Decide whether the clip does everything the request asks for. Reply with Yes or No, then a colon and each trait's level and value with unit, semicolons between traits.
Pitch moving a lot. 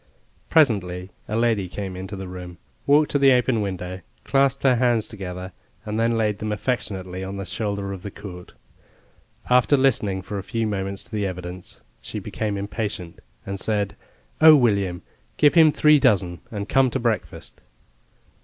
No: average, 4.2 semitones